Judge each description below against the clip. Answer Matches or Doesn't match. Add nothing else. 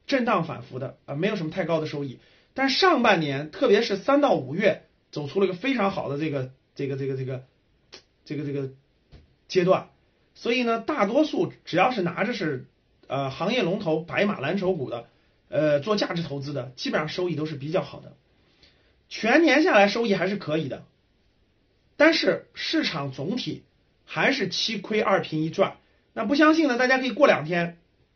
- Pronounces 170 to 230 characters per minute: Doesn't match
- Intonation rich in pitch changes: Matches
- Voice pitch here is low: Doesn't match